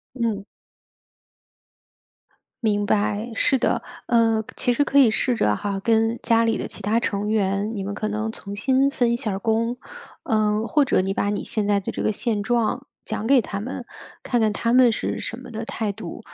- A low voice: No, high, 220 Hz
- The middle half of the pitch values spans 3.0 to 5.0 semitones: No, narrow, 2.5 semitones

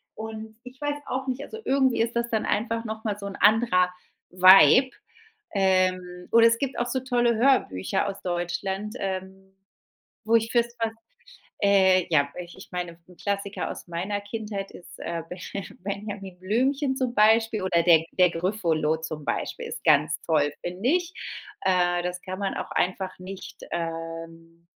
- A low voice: No, high, 195 Hz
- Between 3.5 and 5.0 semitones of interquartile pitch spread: Yes, average, 4.2 semitones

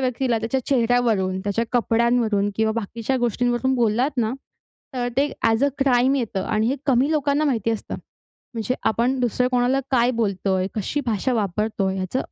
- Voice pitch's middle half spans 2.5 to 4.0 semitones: Yes, average, 2.8 semitones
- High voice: Yes, high, 235 Hz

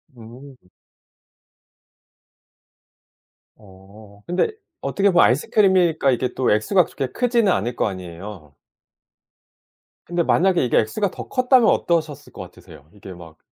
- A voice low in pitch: Yes, low, 130 Hz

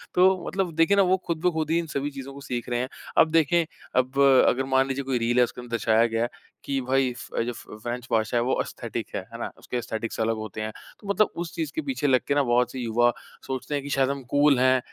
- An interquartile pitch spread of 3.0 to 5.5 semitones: Yes, average, 4.6 semitones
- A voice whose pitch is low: Yes, low, 130 Hz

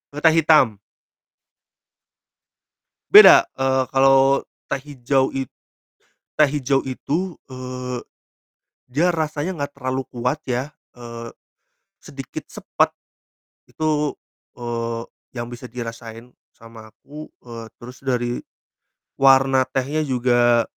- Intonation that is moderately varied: Yes, average, 3.0 semitones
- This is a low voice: Yes, low, 130 Hz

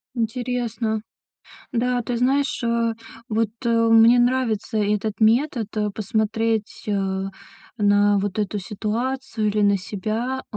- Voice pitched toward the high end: Yes, high, 225 Hz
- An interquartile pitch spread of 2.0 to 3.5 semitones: Yes, narrow, 2.5 semitones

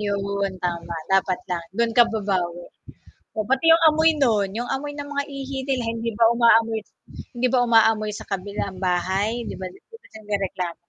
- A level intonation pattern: No, average, 4.1 semitones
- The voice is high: Yes, high, 215 Hz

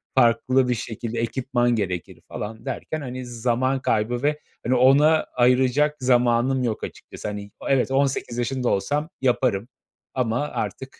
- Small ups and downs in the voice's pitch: Yes, narrow, 2.2 semitones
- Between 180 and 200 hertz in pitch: No, low, 125 Hz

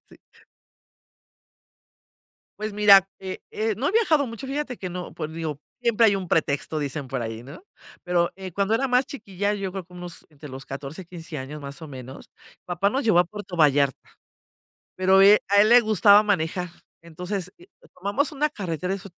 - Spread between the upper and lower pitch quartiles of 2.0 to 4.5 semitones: No, average, 4.9 semitones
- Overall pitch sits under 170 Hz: No, medium, 185 Hz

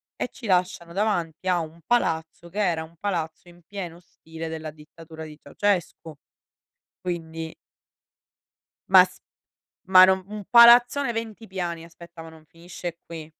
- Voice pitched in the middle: Yes, medium, 170 Hz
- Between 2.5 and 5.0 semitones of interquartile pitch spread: Yes, average, 2.8 semitones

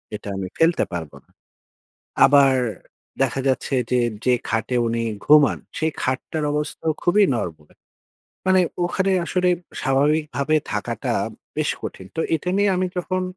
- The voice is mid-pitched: Yes, medium, 145 Hz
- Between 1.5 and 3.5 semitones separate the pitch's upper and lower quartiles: No, wide, 5.5 semitones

